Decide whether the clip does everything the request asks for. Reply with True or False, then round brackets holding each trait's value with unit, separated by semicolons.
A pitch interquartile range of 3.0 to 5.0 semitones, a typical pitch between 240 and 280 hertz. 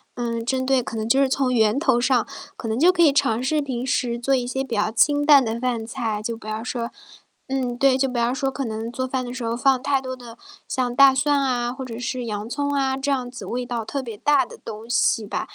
False (2.5 semitones; 250 Hz)